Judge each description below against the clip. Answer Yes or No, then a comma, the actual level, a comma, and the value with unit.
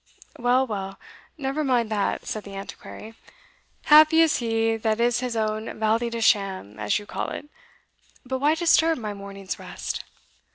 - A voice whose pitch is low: No, high, 225 Hz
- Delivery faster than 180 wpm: No, average, 160 wpm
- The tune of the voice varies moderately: Yes, average, 4.1 semitones